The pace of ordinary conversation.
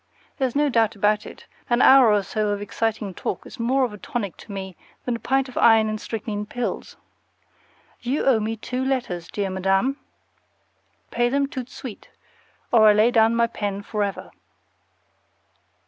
Yes: average, 175 wpm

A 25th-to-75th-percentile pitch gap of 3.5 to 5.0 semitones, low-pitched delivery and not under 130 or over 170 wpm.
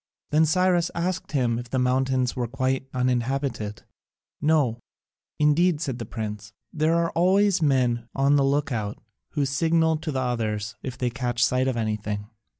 Yes: average, 4.6 semitones; low, 130 Hz; average, 160 wpm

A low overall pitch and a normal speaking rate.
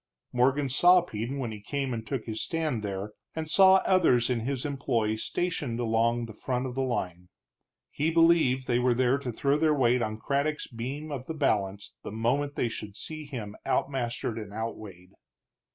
Yes: low, 125 Hz; average, 185 wpm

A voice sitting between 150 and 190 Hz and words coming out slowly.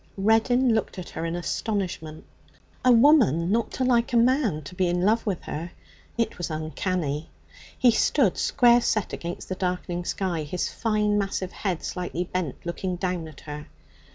No: medium, 185 Hz; average, 170 wpm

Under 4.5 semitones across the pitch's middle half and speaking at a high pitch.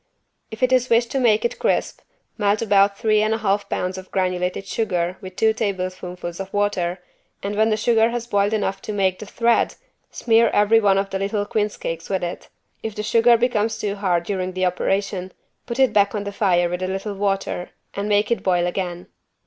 Yes: average, 2.8 semitones; high, 200 Hz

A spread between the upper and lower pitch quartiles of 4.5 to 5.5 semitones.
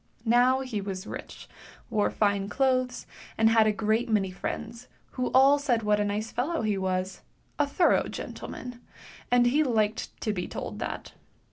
No: average, 3.6 semitones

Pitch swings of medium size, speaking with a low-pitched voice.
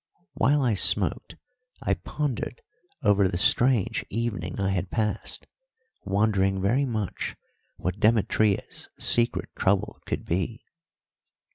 Yes: average, 3.4 semitones; low, 105 Hz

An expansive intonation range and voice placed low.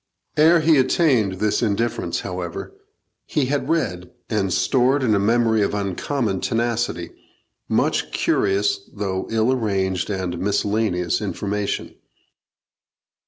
No: average, 4.0 semitones; low, 105 Hz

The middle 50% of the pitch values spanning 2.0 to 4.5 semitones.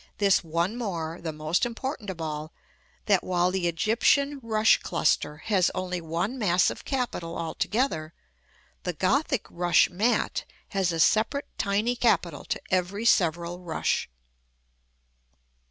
No: average, 4.9 semitones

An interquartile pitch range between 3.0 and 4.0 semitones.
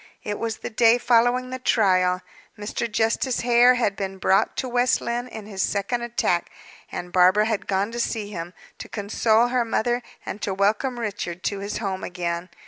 Yes: average, 3.7 semitones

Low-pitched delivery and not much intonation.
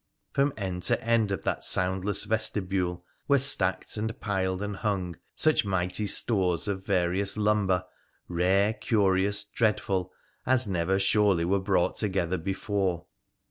Yes: very low, 95 Hz; narrow, 2.3 semitones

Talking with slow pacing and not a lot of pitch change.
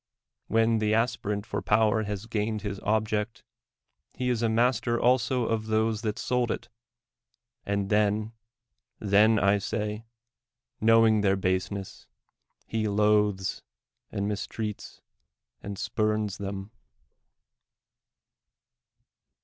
Yes: slow, 105 wpm; narrow, 1.7 semitones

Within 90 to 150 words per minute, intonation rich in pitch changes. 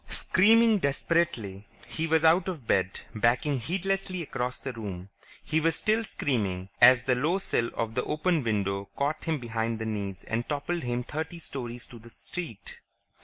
No: average, 170 wpm; wide, 6.7 semitones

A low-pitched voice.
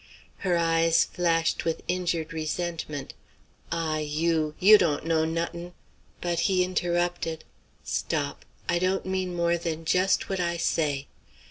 No: medium, 170 Hz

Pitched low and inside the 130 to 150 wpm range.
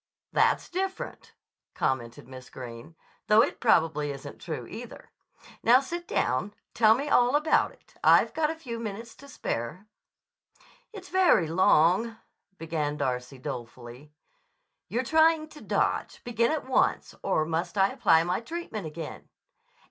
No: high, 195 Hz; average, 140 wpm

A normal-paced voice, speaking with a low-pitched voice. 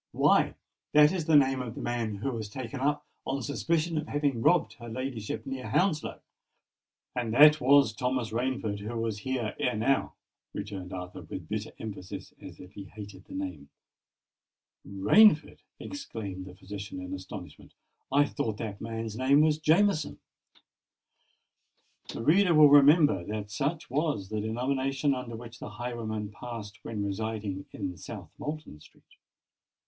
Yes: average, 150 wpm; low, 120 Hz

